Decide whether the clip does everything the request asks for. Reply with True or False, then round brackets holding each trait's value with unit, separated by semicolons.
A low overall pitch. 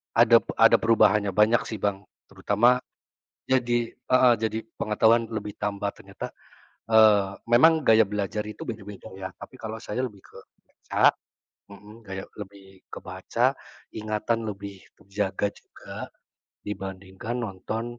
True (105 Hz)